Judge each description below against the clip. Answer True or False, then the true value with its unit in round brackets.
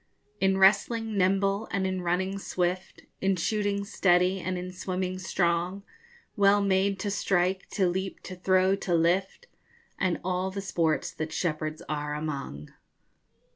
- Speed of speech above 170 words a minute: False (140 wpm)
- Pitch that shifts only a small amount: True (1.8 semitones)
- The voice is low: False (185 Hz)